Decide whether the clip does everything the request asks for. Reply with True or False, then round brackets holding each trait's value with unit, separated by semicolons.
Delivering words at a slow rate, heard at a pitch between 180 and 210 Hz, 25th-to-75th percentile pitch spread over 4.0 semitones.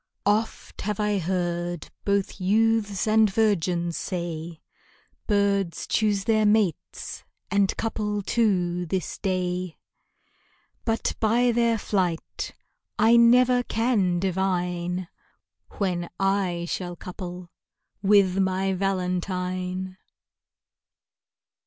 False (90 wpm; 190 Hz; 2.9 semitones)